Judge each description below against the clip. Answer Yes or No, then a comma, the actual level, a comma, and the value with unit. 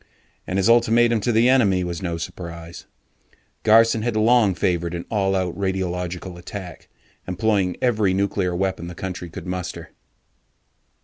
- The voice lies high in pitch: No, very low, 95 Hz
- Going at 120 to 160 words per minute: Yes, average, 140 wpm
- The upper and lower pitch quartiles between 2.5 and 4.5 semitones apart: Yes, average, 3.7 semitones